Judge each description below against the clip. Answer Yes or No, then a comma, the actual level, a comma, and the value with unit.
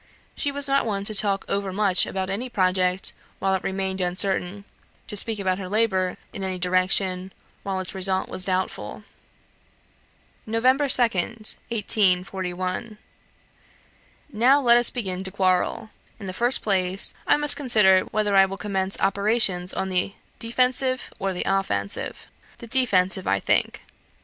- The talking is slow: No, average, 145 wpm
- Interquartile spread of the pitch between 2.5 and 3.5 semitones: Yes, average, 3.1 semitones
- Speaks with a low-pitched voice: No, high, 195 Hz